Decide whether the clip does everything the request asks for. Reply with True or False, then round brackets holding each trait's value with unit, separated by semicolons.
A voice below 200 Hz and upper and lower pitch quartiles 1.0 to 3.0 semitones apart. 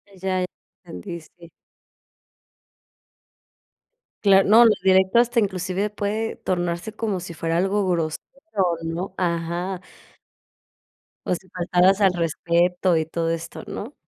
True (185 Hz; 2.6 semitones)